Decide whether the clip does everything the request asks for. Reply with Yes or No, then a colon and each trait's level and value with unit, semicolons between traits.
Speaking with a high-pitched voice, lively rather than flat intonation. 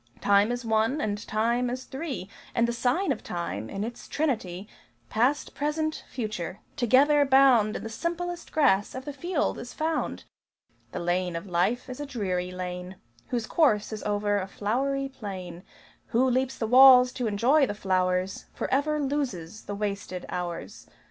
Yes: high, 230 Hz; wide, 5.7 semitones